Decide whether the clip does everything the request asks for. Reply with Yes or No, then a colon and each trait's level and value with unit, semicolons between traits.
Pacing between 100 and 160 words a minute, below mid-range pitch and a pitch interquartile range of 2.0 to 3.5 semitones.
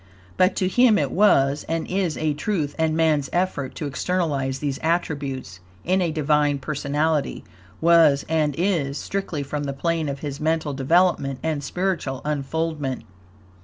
No: average, 150 wpm; medium, 150 Hz; average, 3.2 semitones